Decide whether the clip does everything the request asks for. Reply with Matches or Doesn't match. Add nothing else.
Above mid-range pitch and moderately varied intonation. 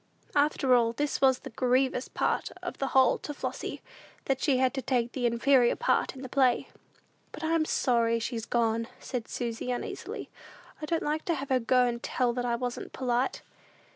Doesn't match